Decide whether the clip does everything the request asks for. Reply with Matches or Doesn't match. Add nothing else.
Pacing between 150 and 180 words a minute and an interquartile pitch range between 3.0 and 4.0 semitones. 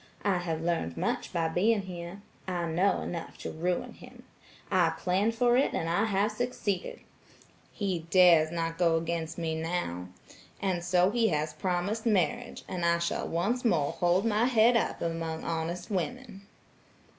Matches